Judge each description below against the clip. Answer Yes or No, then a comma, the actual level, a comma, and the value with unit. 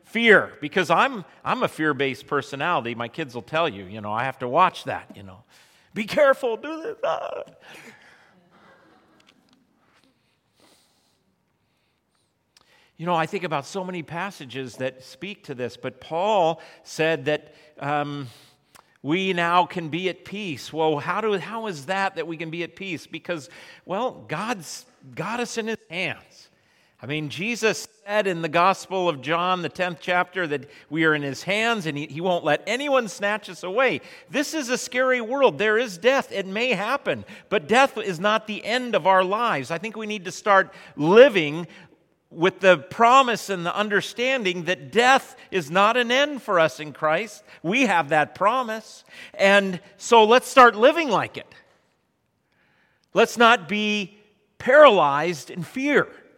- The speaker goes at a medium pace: Yes, average, 165 wpm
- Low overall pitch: No, medium, 185 Hz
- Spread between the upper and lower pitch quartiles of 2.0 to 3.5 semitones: No, wide, 5.6 semitones